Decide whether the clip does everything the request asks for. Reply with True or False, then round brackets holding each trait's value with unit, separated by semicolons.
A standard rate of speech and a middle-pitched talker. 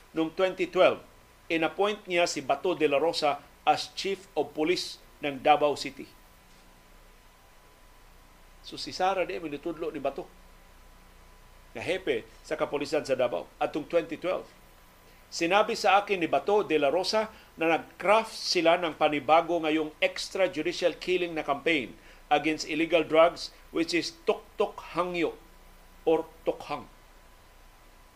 True (120 wpm; 160 Hz)